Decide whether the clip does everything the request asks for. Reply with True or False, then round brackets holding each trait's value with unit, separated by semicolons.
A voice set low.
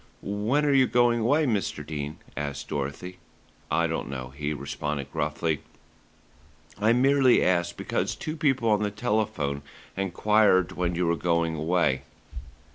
True (90 Hz)